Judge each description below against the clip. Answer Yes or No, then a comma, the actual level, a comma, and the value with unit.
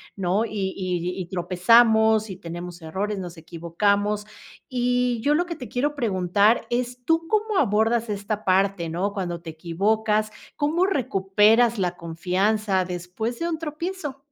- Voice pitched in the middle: No, high, 210 Hz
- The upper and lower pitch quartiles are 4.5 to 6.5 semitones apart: Yes, average, 5.0 semitones